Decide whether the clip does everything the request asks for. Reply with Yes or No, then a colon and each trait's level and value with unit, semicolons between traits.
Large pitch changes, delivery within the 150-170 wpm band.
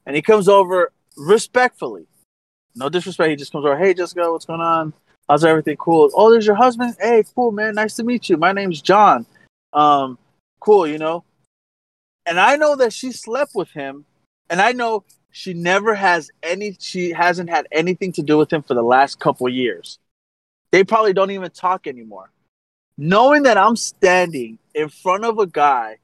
No: wide, 6.2 semitones; average, 185 wpm